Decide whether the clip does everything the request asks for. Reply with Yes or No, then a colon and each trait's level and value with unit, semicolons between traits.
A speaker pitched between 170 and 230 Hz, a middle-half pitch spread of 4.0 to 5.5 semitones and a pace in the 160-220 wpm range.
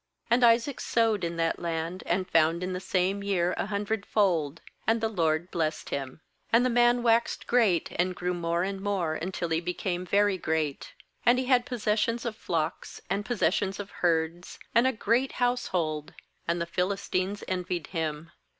Yes: medium, 185 Hz; average, 4.7 semitones; average, 170 wpm